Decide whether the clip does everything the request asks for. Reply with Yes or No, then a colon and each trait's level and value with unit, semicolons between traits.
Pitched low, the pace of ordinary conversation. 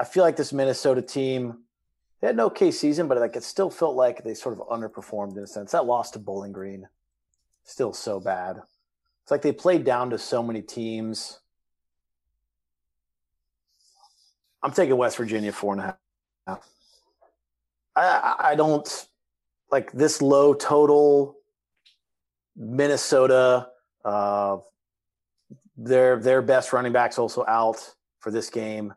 Yes: low, 110 Hz; average, 145 wpm